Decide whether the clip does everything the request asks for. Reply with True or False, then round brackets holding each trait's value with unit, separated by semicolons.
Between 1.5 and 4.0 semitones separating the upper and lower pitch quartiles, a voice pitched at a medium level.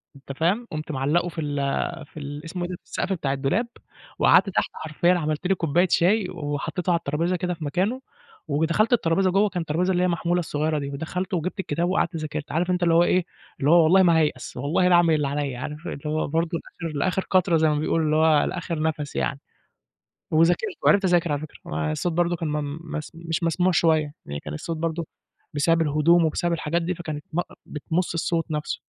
True (2.8 semitones; 165 Hz)